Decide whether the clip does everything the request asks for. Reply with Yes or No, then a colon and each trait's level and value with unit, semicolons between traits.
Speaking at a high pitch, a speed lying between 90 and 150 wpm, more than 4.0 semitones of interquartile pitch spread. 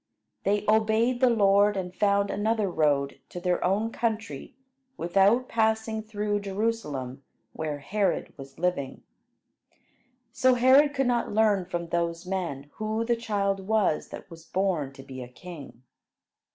Yes: high, 200 Hz; average, 140 wpm; average, 4.7 semitones